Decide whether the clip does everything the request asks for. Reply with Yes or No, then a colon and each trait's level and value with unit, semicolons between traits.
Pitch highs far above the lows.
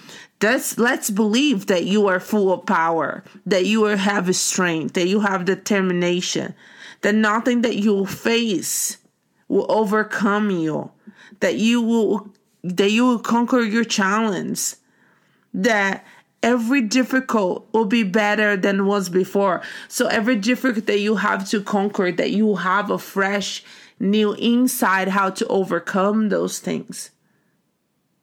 No: average, 2.7 semitones